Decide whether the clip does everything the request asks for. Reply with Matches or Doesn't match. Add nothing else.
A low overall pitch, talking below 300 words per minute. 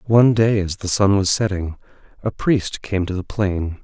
Matches